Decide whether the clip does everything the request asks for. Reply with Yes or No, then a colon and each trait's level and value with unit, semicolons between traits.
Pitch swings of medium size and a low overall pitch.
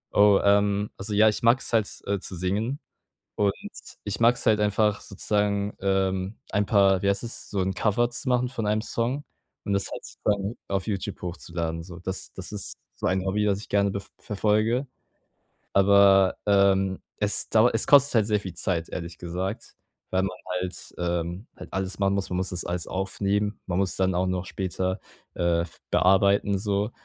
No: narrow, 2.0 semitones; low, 100 Hz